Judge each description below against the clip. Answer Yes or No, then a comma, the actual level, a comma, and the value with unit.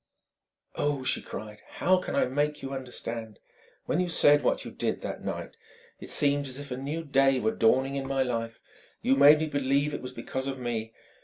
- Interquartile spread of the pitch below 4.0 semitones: Yes, narrow, 2.5 semitones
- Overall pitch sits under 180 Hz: Yes, low, 135 Hz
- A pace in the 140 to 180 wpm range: No, fast, 205 wpm